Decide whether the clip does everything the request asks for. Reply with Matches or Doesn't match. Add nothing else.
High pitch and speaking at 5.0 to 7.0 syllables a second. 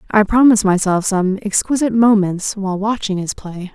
Matches